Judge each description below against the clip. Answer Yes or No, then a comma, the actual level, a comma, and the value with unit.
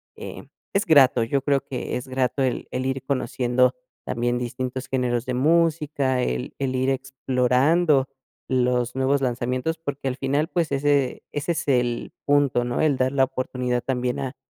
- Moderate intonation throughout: No, narrow, 2.0 semitones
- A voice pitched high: No, low, 130 Hz